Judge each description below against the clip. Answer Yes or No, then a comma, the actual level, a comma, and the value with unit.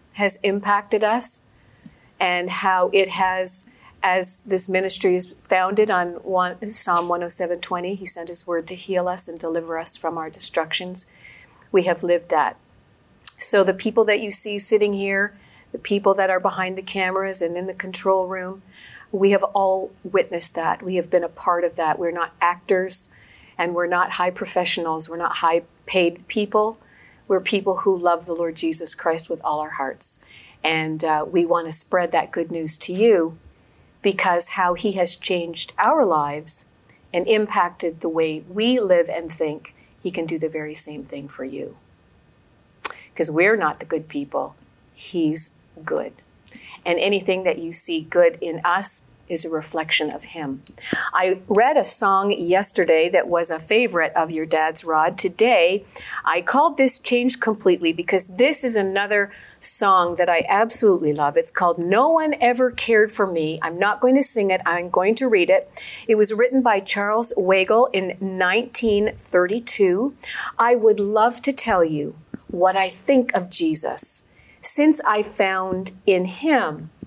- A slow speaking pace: No, average, 170 wpm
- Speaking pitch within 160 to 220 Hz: Yes, medium, 185 Hz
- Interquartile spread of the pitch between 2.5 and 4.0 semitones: Yes, average, 3.6 semitones